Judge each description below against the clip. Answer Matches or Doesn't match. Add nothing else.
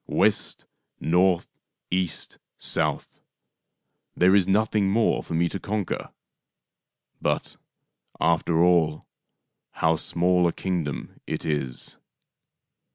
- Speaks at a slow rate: Matches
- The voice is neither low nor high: Doesn't match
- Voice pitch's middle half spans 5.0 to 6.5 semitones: Doesn't match